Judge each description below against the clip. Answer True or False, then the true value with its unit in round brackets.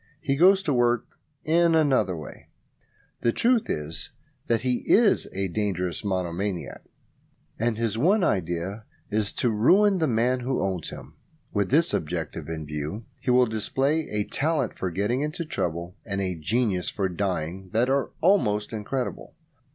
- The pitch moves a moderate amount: False (6.7 semitones)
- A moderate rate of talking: True (155 wpm)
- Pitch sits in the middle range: False (110 Hz)